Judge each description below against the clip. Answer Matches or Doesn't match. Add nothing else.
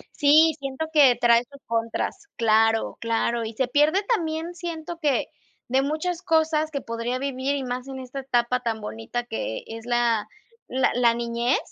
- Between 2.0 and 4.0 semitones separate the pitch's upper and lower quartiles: Doesn't match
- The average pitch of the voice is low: Doesn't match